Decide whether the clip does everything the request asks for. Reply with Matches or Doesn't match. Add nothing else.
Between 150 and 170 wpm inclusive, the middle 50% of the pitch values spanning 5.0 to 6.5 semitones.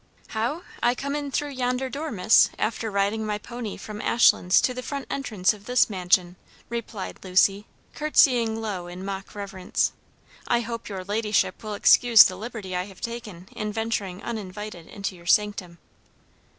Doesn't match